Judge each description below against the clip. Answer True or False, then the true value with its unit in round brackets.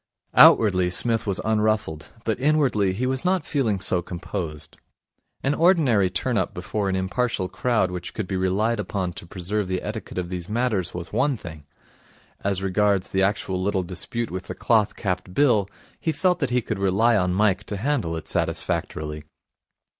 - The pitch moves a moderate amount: True (4.3 semitones)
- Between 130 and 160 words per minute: False (175 wpm)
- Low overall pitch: True (100 Hz)